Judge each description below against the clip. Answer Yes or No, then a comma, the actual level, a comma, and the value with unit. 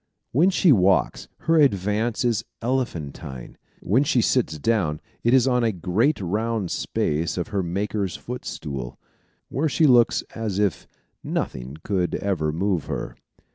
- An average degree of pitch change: No, wide, 5.9 semitones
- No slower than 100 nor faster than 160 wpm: Yes, average, 140 wpm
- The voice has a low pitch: Yes, low, 105 Hz